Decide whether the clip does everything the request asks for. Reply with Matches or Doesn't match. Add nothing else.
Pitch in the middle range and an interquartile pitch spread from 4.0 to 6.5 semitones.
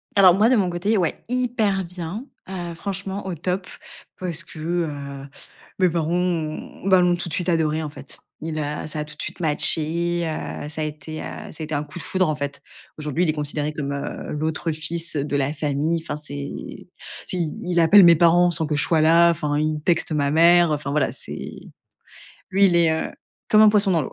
Doesn't match